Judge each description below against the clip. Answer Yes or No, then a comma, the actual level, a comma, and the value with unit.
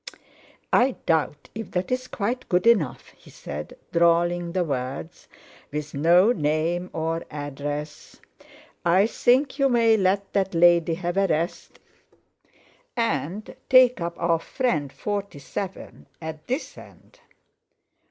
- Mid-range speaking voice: Yes, medium, 175 Hz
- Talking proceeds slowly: Yes, slow, 120 wpm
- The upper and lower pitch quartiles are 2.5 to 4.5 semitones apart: No, average, 4.9 semitones